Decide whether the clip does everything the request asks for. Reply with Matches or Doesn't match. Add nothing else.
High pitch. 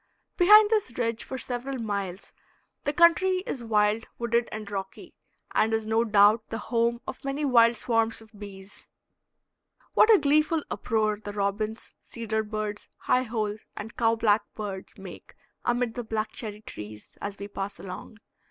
Matches